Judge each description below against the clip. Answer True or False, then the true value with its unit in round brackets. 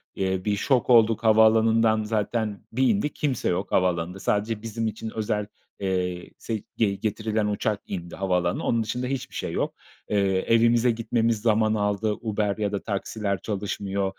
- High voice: False (105 Hz)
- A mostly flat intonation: True (2.3 semitones)